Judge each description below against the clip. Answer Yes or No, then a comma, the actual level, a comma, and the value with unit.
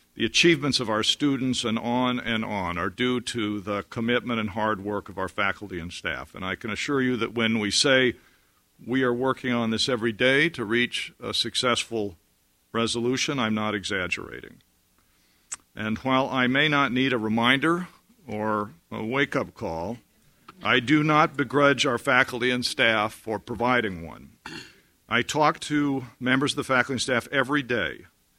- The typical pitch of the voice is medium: No, low, 120 Hz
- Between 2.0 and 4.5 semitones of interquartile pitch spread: Yes, average, 3.5 semitones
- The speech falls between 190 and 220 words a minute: No, average, 170 wpm